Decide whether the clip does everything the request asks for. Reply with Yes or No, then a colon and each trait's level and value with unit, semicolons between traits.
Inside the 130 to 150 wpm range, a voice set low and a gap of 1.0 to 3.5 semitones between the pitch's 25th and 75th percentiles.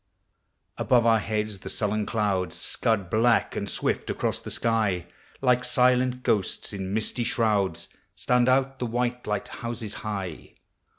Yes: average, 140 wpm; low, 110 Hz; average, 3.1 semitones